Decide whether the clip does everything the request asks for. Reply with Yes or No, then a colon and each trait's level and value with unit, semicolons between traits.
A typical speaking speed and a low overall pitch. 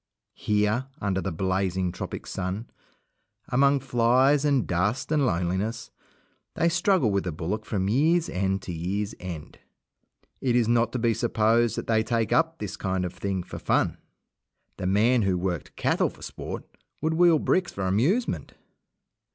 Yes: average, 160 wpm; low, 110 Hz